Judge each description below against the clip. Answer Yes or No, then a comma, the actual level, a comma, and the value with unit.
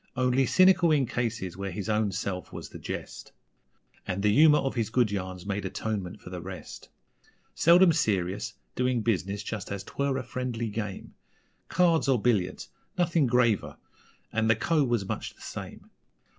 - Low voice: Yes, low, 115 Hz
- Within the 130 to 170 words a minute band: Yes, average, 165 wpm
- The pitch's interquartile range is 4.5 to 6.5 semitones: Yes, average, 5.0 semitones